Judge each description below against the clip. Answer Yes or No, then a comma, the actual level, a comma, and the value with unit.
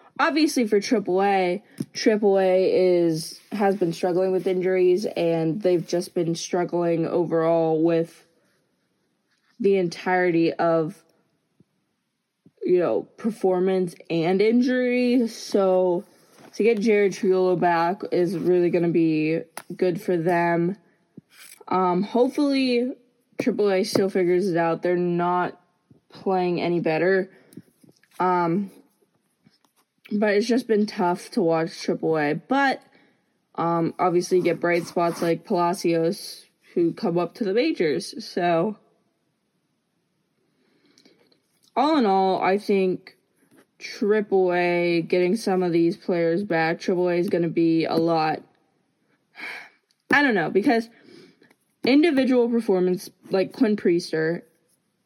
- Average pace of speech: No, slow, 115 wpm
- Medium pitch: Yes, medium, 180 Hz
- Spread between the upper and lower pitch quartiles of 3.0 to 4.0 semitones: Yes, average, 3.5 semitones